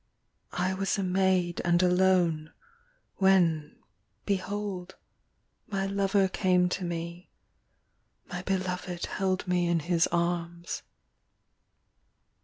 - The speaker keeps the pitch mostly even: Yes, narrow, 1.7 semitones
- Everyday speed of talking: No, slow, 95 wpm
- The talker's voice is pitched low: No, medium, 180 Hz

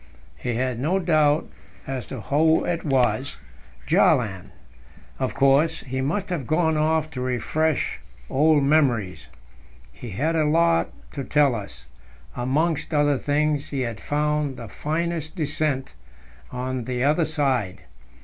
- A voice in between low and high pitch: Yes, medium, 145 Hz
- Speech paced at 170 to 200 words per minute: No, slow, 135 wpm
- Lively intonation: No, average, 3.5 semitones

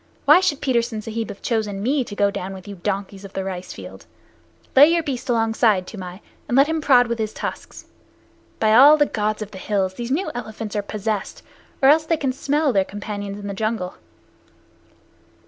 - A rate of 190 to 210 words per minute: Yes, average, 200 wpm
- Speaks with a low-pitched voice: No, high, 220 Hz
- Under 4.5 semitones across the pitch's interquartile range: No, average, 4.8 semitones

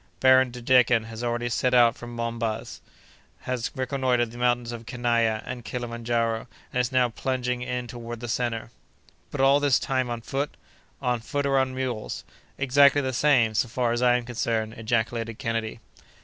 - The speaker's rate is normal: Yes, average, 175 wpm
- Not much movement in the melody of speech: Yes, narrow, 1.8 semitones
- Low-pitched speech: Yes, low, 120 Hz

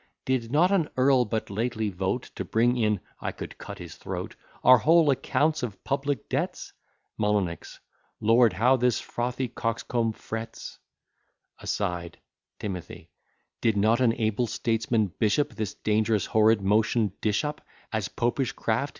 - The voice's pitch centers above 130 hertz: No, low, 115 Hz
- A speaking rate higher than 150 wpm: No, average, 140 wpm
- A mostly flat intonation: No, average, 3.1 semitones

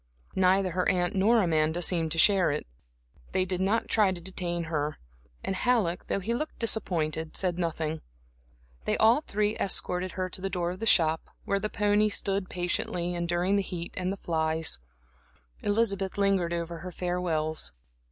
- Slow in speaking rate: No, average, 170 wpm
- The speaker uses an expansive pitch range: No, average, 2.7 semitones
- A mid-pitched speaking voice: Yes, medium, 180 Hz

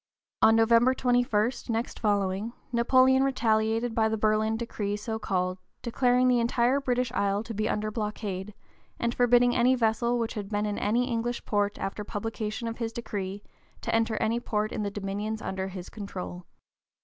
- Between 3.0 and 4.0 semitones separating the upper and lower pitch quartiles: No, narrow, 2.4 semitones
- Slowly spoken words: No, average, 170 wpm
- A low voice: No, high, 220 Hz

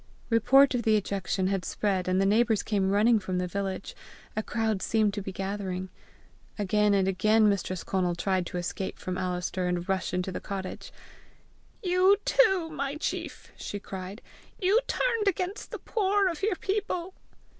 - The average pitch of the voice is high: Yes, high, 205 Hz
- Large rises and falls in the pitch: Yes, wide, 6.9 semitones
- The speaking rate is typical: Yes, average, 165 wpm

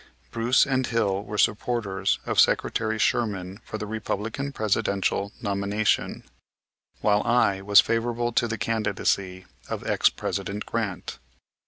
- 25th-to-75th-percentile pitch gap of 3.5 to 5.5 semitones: No, narrow, 2.5 semitones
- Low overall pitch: Yes, low, 105 Hz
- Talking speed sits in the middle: No, slow, 125 wpm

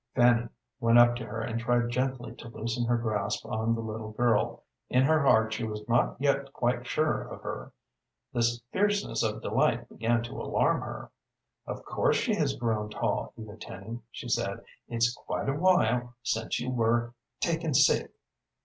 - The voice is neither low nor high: No, low, 120 Hz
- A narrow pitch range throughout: Yes, narrow, 1.8 semitones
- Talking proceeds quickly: No, average, 175 wpm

